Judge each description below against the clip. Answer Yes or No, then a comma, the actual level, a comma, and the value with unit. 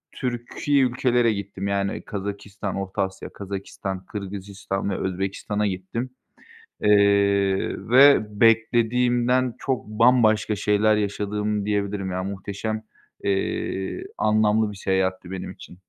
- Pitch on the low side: Yes, low, 105 Hz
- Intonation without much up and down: Yes, narrow, 2.3 semitones